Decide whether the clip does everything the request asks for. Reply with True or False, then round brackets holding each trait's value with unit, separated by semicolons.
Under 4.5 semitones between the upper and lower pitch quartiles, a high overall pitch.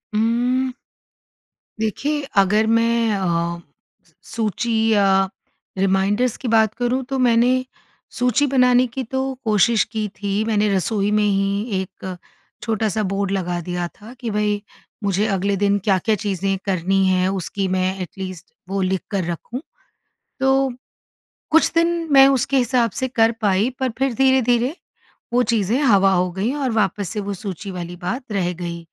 True (4.1 semitones; 210 Hz)